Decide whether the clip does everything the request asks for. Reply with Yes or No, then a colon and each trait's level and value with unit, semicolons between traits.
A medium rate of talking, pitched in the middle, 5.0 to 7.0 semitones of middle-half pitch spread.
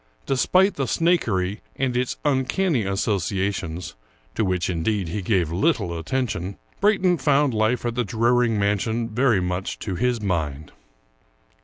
No: average, 150 wpm; low, 110 Hz; wide, 5.6 semitones